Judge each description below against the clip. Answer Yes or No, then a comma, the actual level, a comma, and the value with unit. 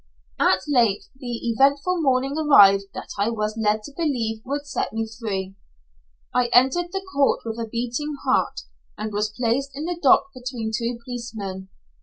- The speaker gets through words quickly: No, average, 165 wpm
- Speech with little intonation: No, average, 4.1 semitones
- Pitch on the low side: No, high, 240 Hz